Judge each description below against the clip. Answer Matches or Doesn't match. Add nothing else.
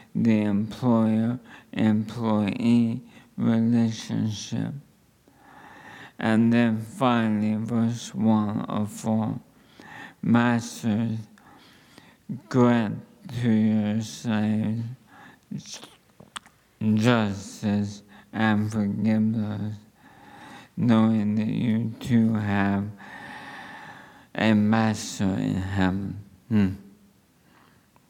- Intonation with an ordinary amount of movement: Doesn't match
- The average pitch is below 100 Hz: Doesn't match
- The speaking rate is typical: Doesn't match